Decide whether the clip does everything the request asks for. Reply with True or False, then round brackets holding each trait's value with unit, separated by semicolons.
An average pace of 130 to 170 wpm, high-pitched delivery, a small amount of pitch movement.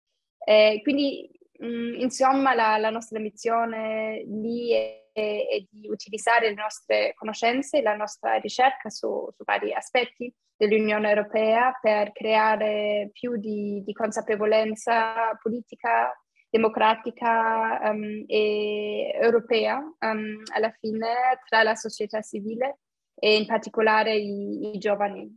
False (115 wpm; 220 Hz; 1.6 semitones)